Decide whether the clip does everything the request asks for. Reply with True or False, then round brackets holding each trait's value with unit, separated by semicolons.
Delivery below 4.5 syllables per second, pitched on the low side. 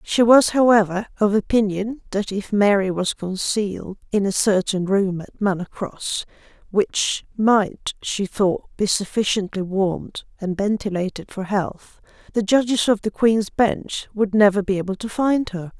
False (4.3 syllables/s; 205 Hz)